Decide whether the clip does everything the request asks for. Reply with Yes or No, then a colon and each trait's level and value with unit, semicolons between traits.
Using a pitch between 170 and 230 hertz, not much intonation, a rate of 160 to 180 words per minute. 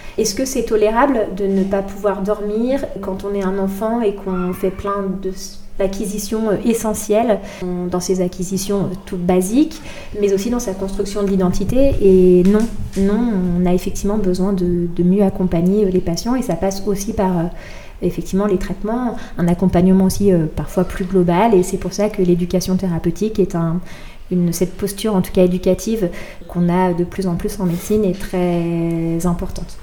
Yes: high, 190 Hz; narrow, 2.3 semitones; average, 175 wpm